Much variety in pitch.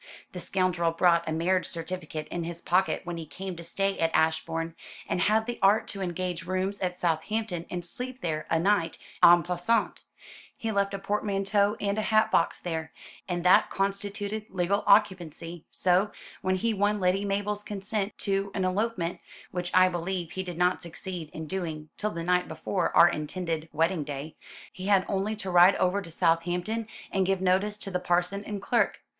No: average, 2.8 semitones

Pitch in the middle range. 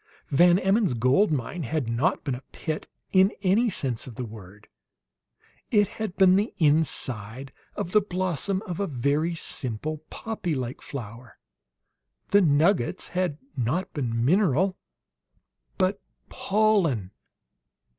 Yes: medium, 160 Hz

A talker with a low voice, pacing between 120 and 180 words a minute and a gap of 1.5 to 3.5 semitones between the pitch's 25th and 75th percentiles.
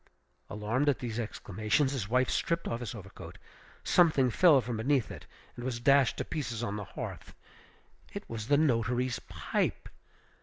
No: low, 120 Hz; average, 160 wpm; average, 3.9 semitones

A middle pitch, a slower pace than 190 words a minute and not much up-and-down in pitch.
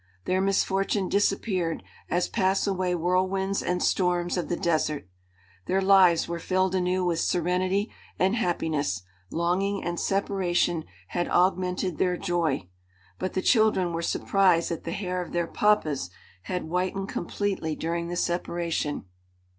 Yes: medium, 180 Hz; average, 140 wpm; narrow, 2.0 semitones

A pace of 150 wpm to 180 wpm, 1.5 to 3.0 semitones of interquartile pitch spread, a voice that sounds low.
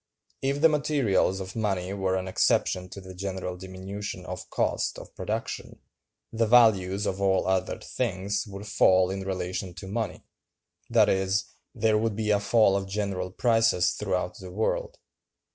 Yes: average, 155 wpm; narrow, 2.4 semitones; very low, 95 Hz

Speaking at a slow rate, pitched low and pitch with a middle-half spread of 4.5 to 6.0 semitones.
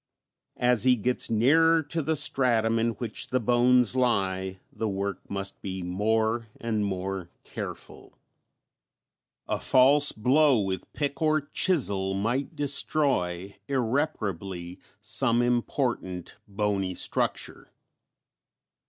Yes: slow, 110 wpm; low, 115 Hz; average, 5.1 semitones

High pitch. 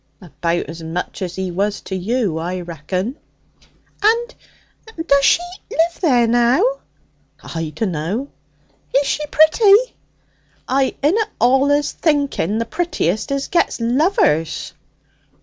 Yes: high, 240 Hz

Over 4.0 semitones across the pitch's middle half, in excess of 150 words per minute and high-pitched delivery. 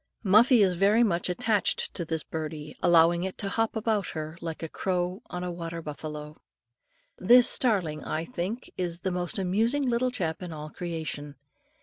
No: average, 4.4 semitones; average, 170 wpm; medium, 180 Hz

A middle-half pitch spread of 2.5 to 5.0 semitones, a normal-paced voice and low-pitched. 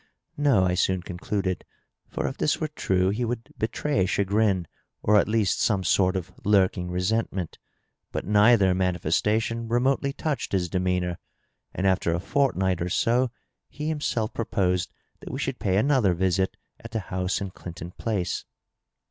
Yes: average, 3.9 semitones; average, 150 wpm; very low, 95 Hz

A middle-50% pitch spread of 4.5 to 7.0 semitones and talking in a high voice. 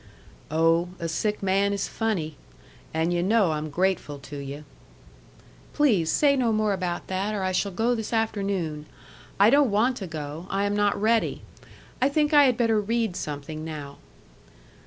Yes: wide, 5.6 semitones; high, 195 Hz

